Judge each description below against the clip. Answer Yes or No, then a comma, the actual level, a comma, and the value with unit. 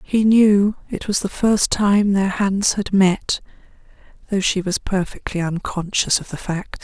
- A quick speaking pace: No, average, 165 wpm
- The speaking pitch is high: Yes, high, 195 Hz